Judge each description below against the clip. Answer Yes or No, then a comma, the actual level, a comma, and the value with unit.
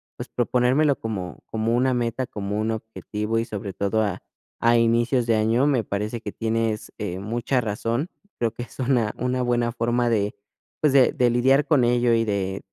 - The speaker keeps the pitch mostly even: Yes, narrow, 2.3 semitones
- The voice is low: Yes, low, 115 Hz